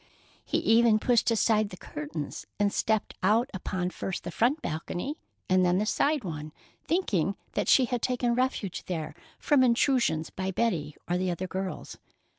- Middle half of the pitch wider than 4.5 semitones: Yes, average, 5.1 semitones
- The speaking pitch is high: Yes, high, 200 Hz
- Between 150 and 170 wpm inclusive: Yes, average, 165 wpm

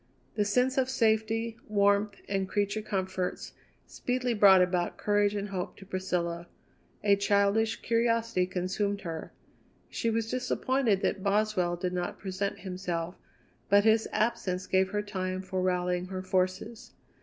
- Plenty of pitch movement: No, average, 2.8 semitones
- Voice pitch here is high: Yes, high, 200 Hz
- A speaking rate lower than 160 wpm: Yes, average, 140 wpm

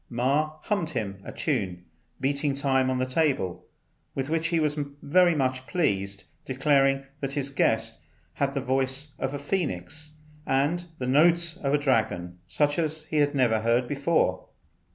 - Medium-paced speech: Yes, average, 160 wpm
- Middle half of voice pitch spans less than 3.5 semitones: Yes, average, 3.1 semitones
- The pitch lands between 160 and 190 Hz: No, medium, 140 Hz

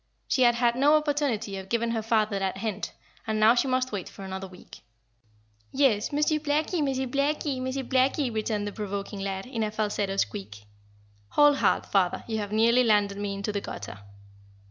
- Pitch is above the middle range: Yes, high, 220 Hz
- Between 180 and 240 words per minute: Yes, average, 185 wpm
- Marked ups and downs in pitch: No, average, 4.5 semitones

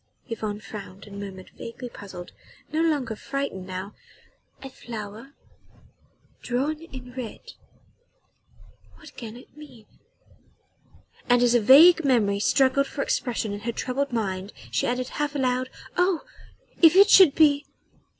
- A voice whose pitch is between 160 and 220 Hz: No, very high, 250 Hz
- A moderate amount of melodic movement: Yes, average, 5.0 semitones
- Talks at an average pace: No, slow, 130 wpm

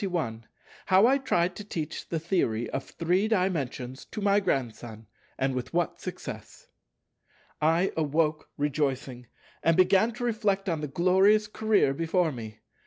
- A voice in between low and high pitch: Yes, medium, 165 Hz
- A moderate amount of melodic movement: No, wide, 6.2 semitones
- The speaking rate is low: No, average, 150 wpm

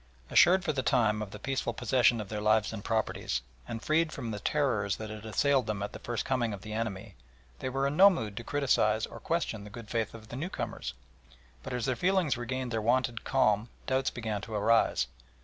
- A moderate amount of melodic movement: Yes, average, 3.6 semitones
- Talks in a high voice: No, low, 115 Hz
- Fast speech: Yes, fast, 220 wpm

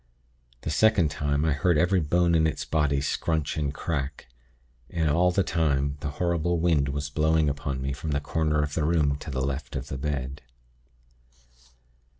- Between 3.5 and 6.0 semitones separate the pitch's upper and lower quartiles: No, narrow, 2.4 semitones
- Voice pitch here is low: Yes, very low, 75 Hz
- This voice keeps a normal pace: Yes, average, 175 wpm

